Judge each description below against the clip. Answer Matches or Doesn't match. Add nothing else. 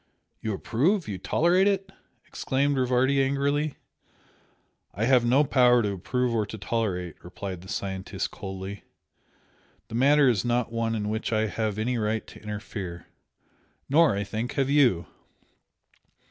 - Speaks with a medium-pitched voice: Doesn't match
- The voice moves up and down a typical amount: Matches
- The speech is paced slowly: Doesn't match